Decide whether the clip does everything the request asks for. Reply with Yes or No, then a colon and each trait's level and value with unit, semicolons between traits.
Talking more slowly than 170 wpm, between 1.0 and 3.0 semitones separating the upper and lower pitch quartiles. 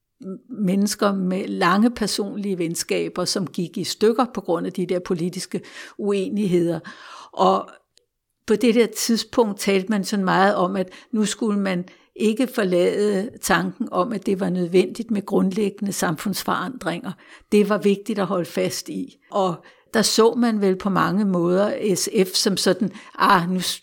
Yes: average, 155 wpm; narrow, 2.6 semitones